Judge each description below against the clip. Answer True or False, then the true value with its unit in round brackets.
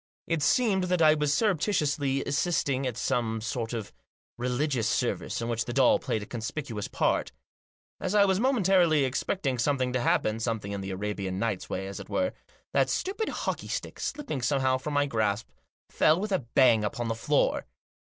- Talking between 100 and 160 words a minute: False (180 wpm)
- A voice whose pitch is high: False (130 Hz)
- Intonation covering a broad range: True (6.1 semitones)